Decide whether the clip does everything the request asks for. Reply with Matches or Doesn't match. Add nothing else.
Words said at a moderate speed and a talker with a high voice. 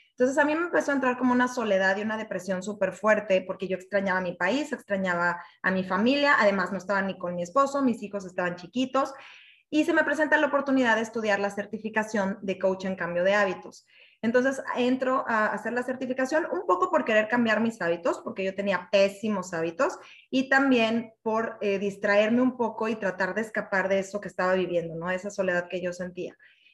Doesn't match